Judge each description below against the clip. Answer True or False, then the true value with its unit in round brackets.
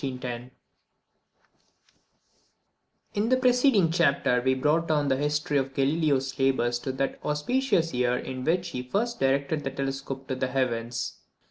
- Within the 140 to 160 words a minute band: True (145 wpm)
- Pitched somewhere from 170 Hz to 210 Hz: False (135 Hz)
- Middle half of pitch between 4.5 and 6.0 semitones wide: False (3.8 semitones)